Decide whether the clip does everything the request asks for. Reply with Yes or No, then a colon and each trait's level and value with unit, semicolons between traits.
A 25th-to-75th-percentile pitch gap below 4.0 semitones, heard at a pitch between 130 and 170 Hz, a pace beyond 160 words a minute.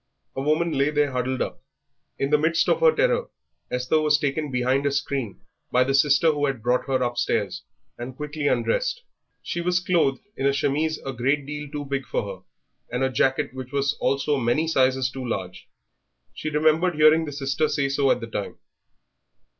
Yes: average, 2.9 semitones; medium, 140 Hz; average, 190 wpm